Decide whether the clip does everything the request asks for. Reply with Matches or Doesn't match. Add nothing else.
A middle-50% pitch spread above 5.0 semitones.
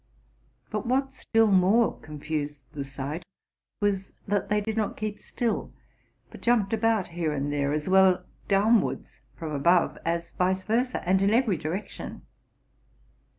Matches